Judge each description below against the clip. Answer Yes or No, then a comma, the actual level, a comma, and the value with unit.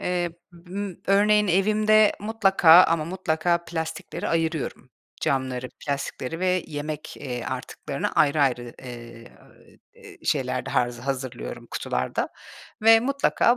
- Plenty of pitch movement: Yes, wide, 6.7 semitones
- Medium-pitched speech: Yes, medium, 165 Hz